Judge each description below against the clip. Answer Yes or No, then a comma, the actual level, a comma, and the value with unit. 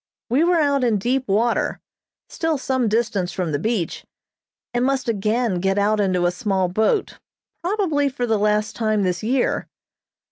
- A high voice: Yes, high, 220 Hz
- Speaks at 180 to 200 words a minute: No, average, 165 wpm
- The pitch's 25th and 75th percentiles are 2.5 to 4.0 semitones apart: No, average, 4.9 semitones